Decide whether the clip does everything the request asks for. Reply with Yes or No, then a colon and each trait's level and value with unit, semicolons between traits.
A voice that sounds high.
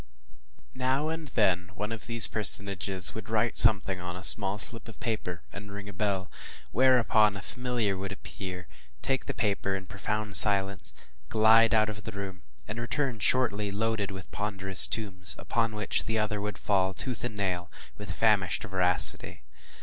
No: low, 105 Hz